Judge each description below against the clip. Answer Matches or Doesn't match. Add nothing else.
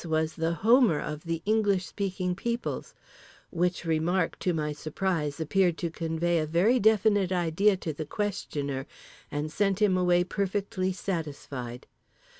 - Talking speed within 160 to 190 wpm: Doesn't match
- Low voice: Doesn't match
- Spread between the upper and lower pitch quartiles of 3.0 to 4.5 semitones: Matches